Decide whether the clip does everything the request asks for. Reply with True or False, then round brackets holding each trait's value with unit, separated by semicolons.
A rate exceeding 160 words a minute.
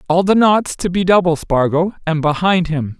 True (200 wpm)